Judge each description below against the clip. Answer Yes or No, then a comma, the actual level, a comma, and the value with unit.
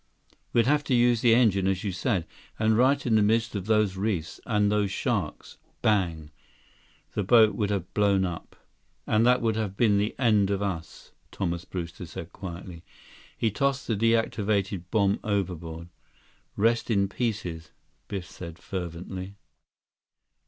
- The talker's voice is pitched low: Yes, low, 100 Hz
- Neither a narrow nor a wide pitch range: Yes, average, 3.4 semitones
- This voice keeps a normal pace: Yes, average, 150 wpm